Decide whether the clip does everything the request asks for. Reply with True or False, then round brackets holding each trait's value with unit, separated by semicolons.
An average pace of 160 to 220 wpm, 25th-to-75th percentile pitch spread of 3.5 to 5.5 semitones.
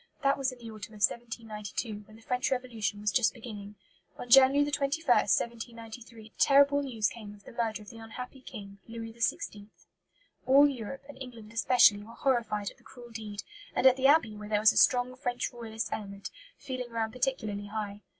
False (190 wpm; 3.1 semitones)